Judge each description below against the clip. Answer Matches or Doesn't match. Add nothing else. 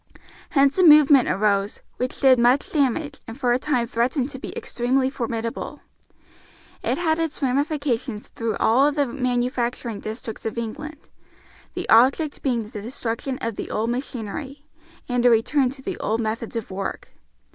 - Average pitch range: Matches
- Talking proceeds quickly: Doesn't match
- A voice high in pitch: Matches